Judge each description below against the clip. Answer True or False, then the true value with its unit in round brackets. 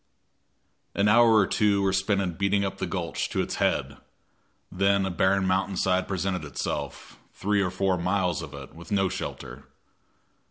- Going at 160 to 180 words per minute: True (170 wpm)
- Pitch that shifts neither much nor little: False (1.5 semitones)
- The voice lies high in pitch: False (95 Hz)